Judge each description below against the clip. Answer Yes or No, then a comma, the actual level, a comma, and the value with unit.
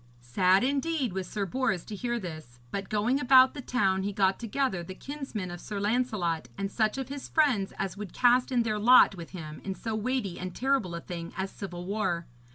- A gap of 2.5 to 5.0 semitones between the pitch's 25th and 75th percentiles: No, wide, 5.4 semitones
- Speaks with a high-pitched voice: Yes, high, 205 Hz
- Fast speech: Yes, fast, 210 wpm